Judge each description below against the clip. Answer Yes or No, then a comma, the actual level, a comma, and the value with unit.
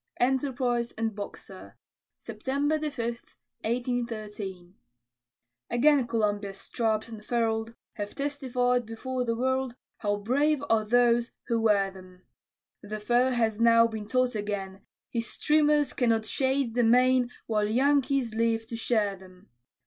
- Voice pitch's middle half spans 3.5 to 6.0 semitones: No, average, 3.0 semitones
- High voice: Yes, high, 230 Hz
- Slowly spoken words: Yes, slow, 125 wpm